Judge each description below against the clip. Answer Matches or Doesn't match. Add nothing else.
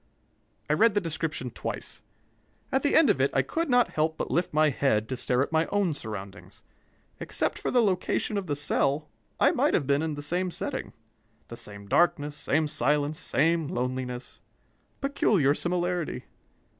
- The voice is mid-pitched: Matches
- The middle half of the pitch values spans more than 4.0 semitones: Matches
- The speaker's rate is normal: Matches